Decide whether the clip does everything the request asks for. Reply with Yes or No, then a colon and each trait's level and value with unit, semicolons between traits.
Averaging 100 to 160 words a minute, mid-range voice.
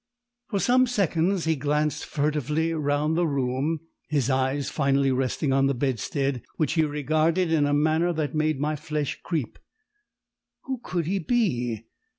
Yes: average, 155 wpm; medium, 150 Hz